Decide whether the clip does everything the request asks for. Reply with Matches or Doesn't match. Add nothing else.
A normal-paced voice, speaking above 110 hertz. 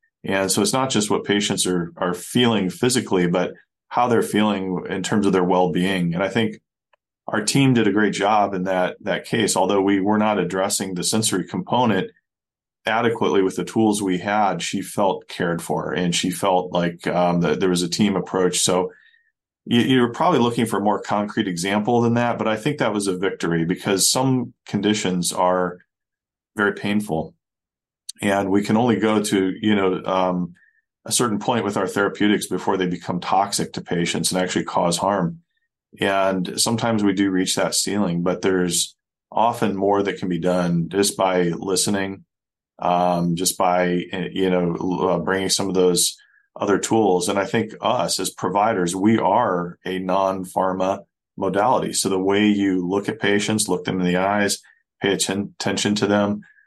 Doesn't match